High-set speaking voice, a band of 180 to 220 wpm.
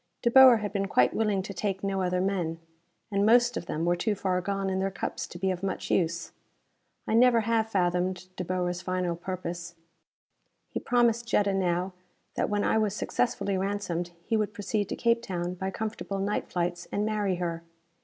Yes: high, 195 Hz; average, 195 wpm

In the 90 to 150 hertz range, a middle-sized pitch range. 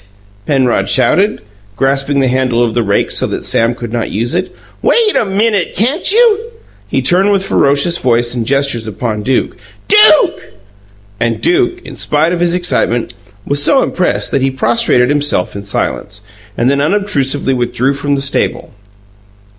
No: medium, 140 Hz; wide, 8.0 semitones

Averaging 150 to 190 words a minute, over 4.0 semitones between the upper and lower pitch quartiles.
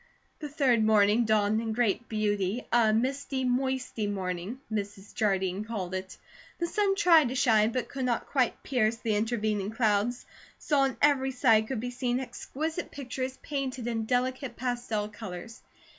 No: average, 160 wpm; average, 3.6 semitones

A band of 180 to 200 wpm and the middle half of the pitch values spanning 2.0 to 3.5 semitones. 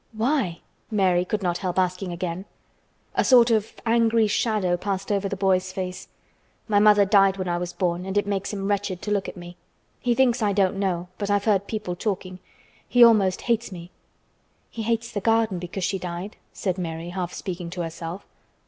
Yes: average, 195 wpm; average, 2.9 semitones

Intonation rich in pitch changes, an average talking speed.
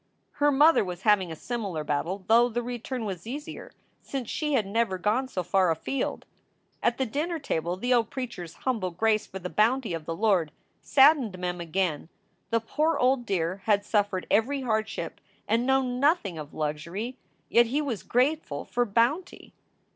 Yes: wide, 5.8 semitones; average, 175 wpm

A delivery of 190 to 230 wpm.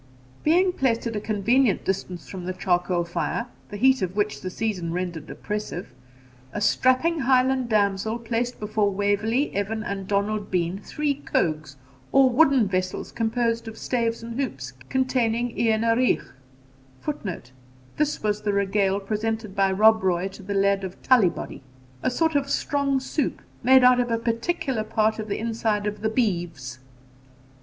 No: average, 155 wpm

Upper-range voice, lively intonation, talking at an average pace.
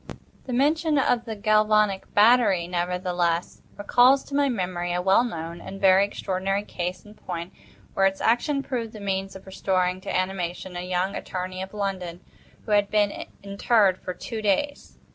No: high, 195 Hz; average, 3.1 semitones; average, 165 wpm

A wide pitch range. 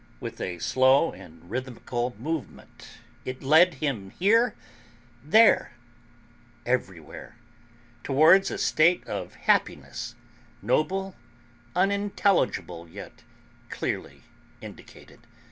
Yes: wide, 7.6 semitones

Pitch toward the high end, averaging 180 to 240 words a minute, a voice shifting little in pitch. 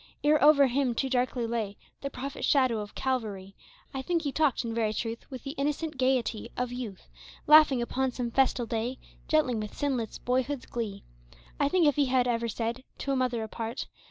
No: very high, 250 Hz; average, 190 wpm; average, 3.2 semitones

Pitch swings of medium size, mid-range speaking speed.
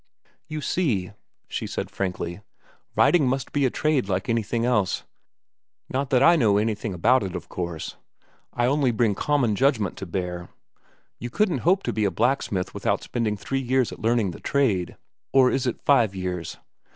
No: wide, 5.8 semitones; average, 170 wpm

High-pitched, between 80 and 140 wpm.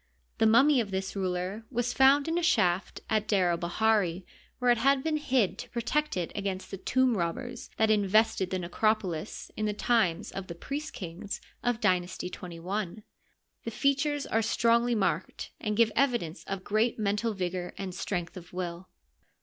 No: high, 210 Hz; average, 180 wpm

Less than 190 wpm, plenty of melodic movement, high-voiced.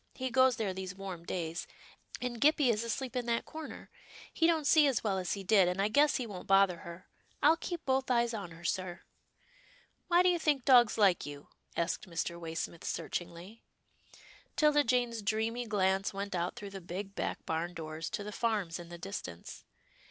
No: average, 200 wpm; wide, 6.0 semitones; high, 205 Hz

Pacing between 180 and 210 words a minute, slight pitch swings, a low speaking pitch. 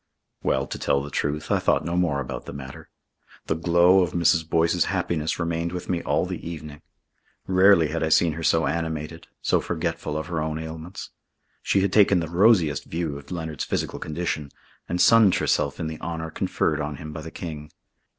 Yes: average, 195 wpm; narrow, 2.1 semitones; very low, 80 Hz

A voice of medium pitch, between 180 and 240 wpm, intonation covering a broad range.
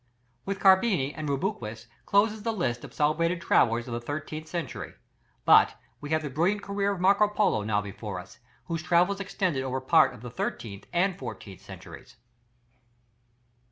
No: medium, 155 Hz; average, 160 wpm; wide, 7.9 semitones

